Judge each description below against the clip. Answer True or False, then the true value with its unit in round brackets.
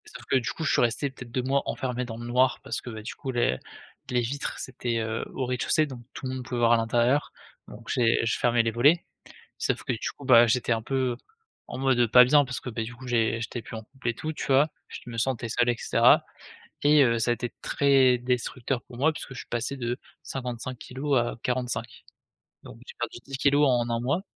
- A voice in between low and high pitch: False (125 Hz)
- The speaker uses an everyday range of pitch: False (2.1 semitones)